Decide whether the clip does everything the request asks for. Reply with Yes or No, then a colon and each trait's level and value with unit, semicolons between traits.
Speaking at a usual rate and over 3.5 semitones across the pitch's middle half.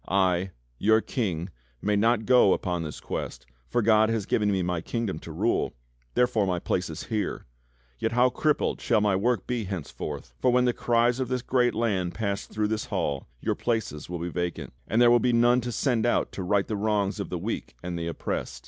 No: fast, 215 wpm; average, 4.6 semitones